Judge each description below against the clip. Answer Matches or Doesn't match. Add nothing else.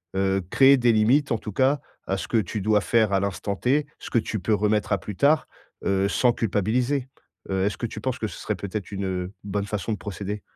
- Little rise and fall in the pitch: Doesn't match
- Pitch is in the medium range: Doesn't match